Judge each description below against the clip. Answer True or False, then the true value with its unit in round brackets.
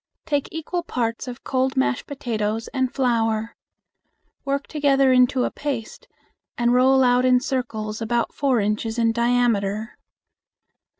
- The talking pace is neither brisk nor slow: False (130 wpm)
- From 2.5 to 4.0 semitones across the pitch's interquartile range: True (2.8 semitones)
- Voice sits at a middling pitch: False (245 Hz)